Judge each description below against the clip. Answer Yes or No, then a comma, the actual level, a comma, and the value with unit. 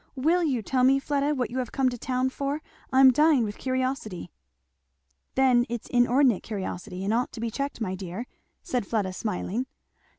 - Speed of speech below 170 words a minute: No, average, 185 wpm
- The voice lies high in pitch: Yes, very high, 250 Hz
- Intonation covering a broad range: No, average, 3.6 semitones